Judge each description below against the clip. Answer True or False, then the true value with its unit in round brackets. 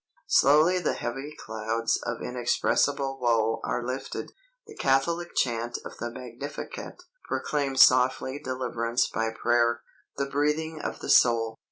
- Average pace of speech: False (130 wpm)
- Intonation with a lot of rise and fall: False (3.3 semitones)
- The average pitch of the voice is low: True (125 Hz)